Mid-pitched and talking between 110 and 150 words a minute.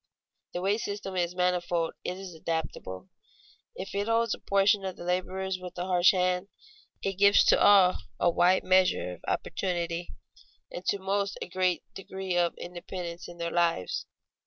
No: medium, 180 Hz; average, 165 wpm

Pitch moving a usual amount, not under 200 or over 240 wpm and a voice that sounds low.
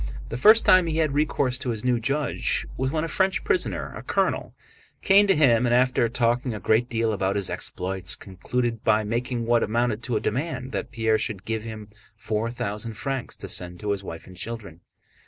Yes: average, 3.6 semitones; fast, 205 wpm; low, 115 Hz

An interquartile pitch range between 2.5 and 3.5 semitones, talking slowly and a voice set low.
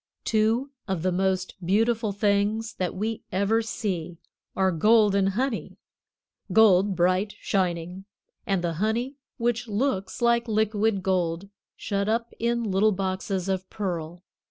No: average, 3.1 semitones; slow, 130 wpm; high, 200 Hz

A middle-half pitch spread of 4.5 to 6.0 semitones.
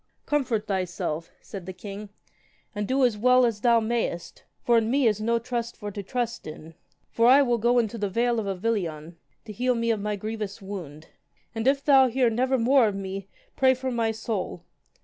No: average, 3.5 semitones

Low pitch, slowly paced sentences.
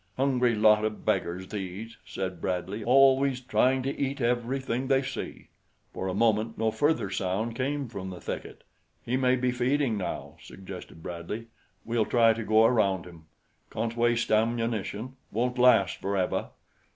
No: low, 115 Hz; average, 150 wpm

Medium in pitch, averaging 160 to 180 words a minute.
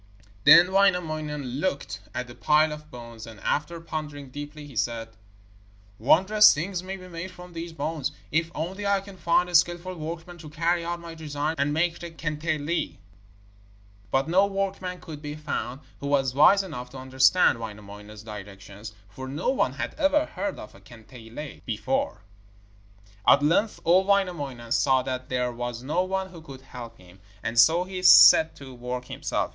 Yes: medium, 150 Hz; average, 170 wpm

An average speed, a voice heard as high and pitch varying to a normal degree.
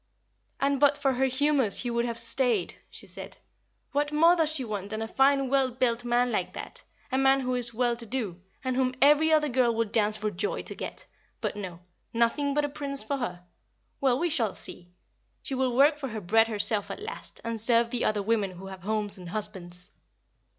No: fast, 215 wpm; high, 240 Hz; average, 4.2 semitones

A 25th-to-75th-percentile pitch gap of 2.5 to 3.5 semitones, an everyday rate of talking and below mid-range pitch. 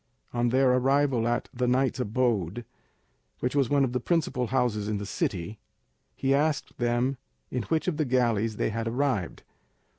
Yes: average, 2.9 semitones; average, 170 wpm; low, 125 Hz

